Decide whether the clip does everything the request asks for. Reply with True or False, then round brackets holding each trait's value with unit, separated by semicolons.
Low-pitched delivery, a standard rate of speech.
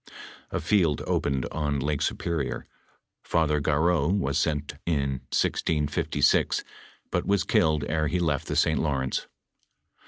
False (75 Hz; 125 wpm)